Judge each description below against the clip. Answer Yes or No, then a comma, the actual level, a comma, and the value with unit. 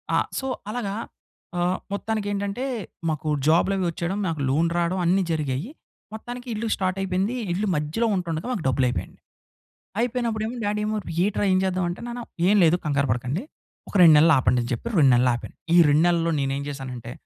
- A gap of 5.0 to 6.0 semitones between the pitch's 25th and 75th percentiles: Yes, wide, 5.6 semitones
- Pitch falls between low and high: Yes, medium, 175 Hz